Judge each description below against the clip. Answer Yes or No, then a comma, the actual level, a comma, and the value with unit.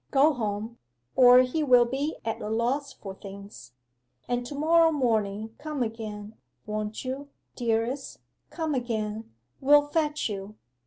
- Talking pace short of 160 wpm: Yes, average, 140 wpm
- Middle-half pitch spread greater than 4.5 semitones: Yes, average, 4.9 semitones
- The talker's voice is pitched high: Yes, high, 240 Hz